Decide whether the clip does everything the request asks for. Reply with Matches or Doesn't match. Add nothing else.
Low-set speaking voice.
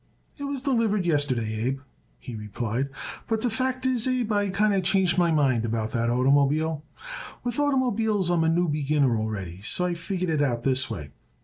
Doesn't match